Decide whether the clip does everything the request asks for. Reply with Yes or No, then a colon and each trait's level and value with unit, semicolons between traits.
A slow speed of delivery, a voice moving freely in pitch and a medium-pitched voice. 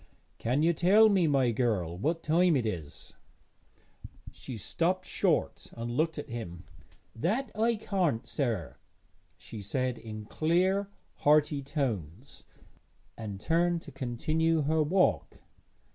Yes: slow, 125 wpm; wide, 6.8 semitones; medium, 145 Hz